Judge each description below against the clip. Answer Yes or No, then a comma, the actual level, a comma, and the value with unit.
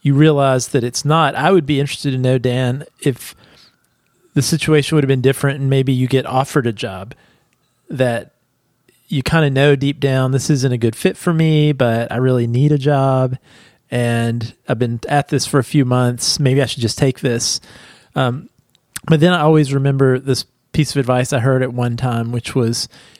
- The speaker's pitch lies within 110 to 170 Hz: Yes, low, 135 Hz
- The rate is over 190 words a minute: Yes, average, 200 wpm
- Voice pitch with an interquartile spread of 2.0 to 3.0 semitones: Yes, narrow, 2.6 semitones